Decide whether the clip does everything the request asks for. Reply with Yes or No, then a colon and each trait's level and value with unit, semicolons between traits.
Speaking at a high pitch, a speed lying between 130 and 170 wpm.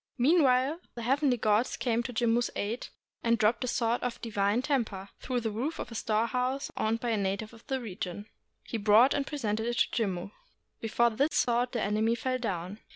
No: high, 235 Hz; average, 200 wpm